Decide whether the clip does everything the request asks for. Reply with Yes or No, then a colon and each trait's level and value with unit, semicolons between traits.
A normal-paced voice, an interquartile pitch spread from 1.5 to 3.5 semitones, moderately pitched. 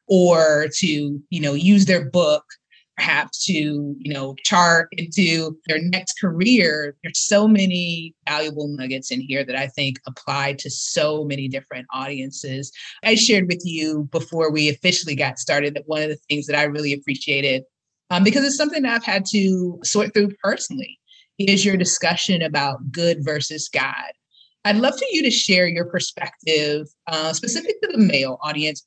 No: average, 170 wpm; average, 4.9 semitones; medium, 160 Hz